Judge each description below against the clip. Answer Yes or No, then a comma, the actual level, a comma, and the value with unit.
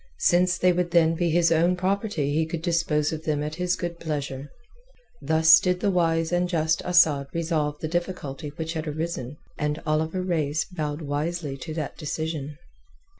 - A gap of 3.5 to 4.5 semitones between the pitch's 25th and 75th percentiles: No, narrow, 2.5 semitones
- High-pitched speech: No, medium, 160 Hz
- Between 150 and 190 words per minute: Yes, average, 175 wpm